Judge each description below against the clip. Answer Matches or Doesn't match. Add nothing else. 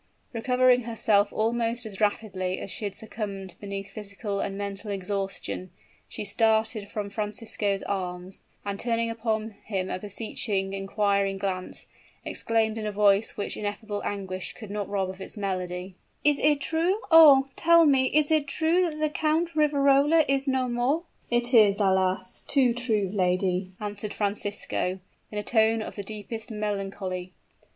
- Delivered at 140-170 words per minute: Matches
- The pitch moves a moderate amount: Matches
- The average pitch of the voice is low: Doesn't match